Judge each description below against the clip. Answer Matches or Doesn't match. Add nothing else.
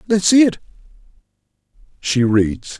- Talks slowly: Matches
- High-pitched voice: Doesn't match